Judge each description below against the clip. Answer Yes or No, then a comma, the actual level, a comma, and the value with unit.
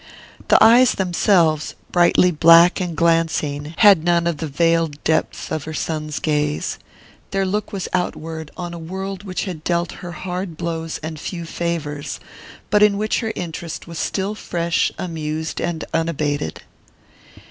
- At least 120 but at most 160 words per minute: Yes, average, 150 wpm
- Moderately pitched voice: Yes, medium, 170 Hz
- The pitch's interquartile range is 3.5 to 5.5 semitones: No, narrow, 2.5 semitones